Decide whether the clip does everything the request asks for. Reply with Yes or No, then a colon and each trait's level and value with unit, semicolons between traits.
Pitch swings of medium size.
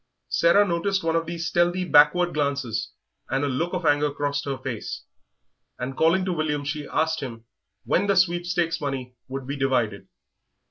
Yes: average, 3.9 semitones